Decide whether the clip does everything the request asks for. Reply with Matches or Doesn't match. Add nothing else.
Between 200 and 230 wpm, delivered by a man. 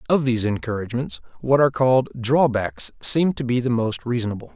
Doesn't match